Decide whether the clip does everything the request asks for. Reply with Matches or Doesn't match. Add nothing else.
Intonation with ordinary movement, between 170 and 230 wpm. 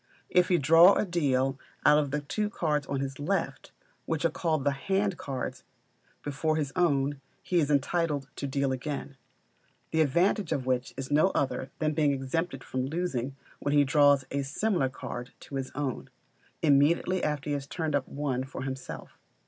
Matches